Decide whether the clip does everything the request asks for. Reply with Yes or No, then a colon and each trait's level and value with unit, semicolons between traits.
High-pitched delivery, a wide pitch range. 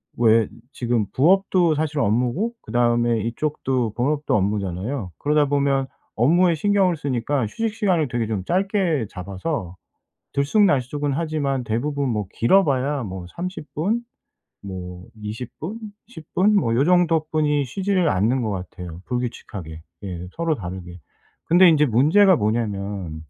No: low, 135 Hz; wide, 7.2 semitones